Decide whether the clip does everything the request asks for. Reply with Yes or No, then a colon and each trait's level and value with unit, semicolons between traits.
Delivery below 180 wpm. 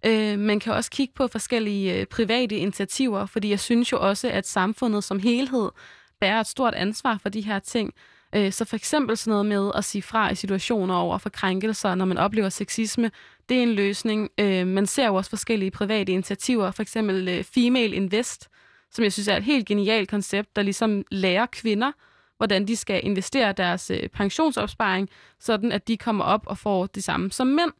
No: average, 185 wpm